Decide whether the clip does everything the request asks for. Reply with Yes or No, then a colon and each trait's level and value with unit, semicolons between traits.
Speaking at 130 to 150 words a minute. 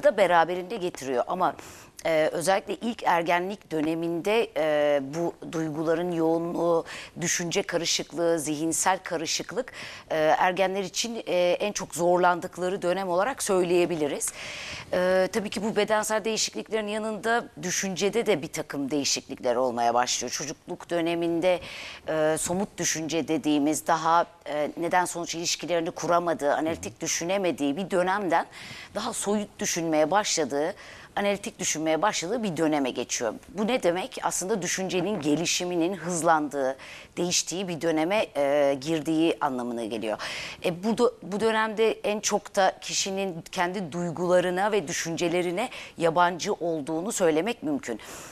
No: average, 120 wpm